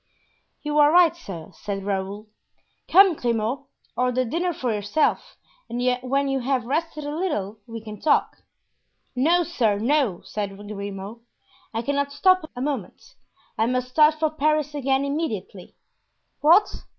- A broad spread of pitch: Yes, wide, 6.1 semitones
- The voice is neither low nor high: No, very high, 265 Hz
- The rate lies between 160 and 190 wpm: No, average, 140 wpm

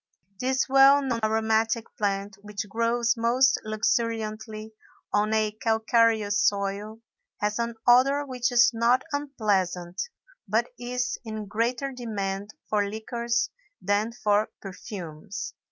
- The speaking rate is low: Yes, slow, 115 wpm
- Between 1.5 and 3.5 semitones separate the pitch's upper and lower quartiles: Yes, narrow, 2.5 semitones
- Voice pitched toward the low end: No, high, 220 Hz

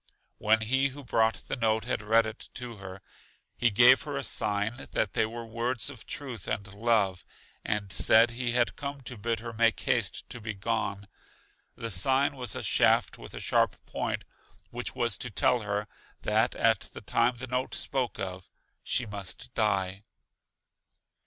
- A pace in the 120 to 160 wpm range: No, average, 175 wpm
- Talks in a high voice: No, low, 115 Hz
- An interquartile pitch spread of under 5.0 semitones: Yes, average, 3.0 semitones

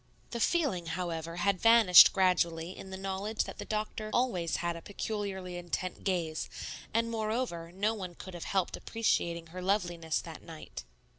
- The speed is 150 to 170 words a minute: Yes, average, 160 wpm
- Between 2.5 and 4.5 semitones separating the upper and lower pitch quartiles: Yes, average, 3.8 semitones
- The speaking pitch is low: No, medium, 185 Hz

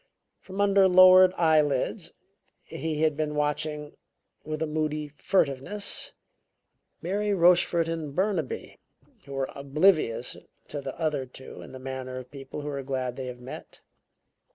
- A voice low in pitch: No, medium, 150 Hz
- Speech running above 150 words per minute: No, average, 140 wpm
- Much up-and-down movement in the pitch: No, average, 4.1 semitones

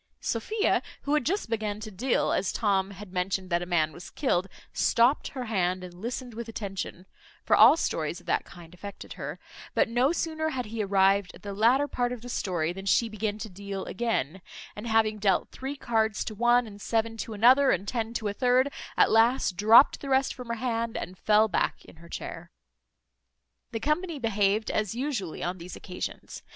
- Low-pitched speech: No, high, 220 Hz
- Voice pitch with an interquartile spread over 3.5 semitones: Yes, average, 4.1 semitones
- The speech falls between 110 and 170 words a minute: No, average, 200 wpm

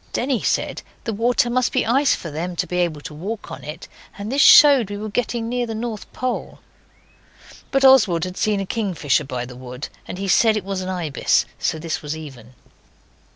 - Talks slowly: No, fast, 205 wpm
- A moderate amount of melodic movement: No, wide, 6.7 semitones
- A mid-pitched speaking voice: No, high, 195 Hz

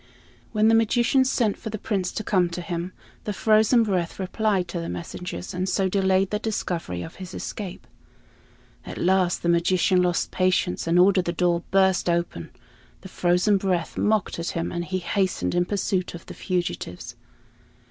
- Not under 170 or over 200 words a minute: Yes, average, 175 wpm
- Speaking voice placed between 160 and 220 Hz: Yes, medium, 185 Hz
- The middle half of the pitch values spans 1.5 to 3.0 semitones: Yes, narrow, 2.5 semitones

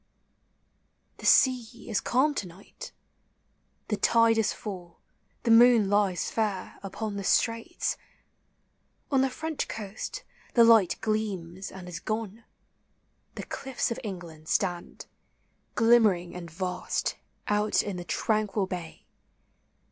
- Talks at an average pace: No, slow, 125 wpm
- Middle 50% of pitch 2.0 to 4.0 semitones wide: Yes, average, 3.7 semitones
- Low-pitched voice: No, high, 210 Hz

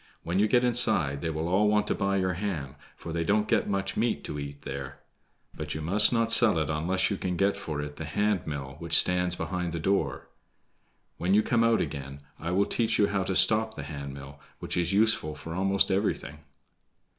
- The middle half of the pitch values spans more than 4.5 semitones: Yes, average, 5.2 semitones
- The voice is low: Yes, very low, 90 Hz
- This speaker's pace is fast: Yes, fast, 215 wpm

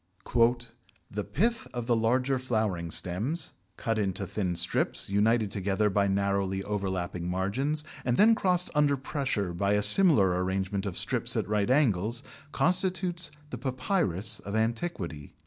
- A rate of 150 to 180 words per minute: No, average, 140 wpm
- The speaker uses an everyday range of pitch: No, wide, 6.0 semitones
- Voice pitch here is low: Yes, low, 105 Hz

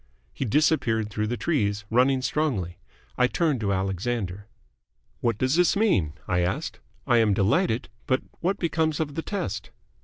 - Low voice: Yes, low, 120 Hz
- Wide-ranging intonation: Yes, wide, 7.3 semitones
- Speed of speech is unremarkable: Yes, average, 155 wpm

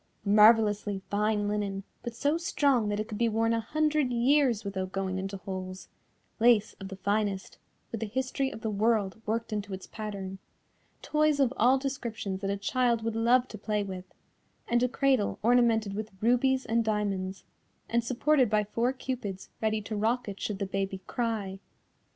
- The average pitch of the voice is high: Yes, high, 220 Hz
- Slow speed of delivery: No, average, 175 wpm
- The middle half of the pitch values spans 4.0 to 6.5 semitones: No, average, 3.3 semitones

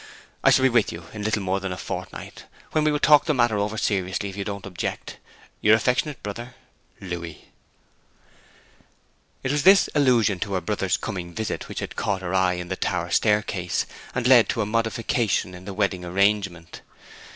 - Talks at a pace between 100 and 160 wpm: No, average, 185 wpm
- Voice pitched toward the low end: Yes, low, 100 Hz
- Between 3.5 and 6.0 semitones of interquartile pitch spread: Yes, average, 4.1 semitones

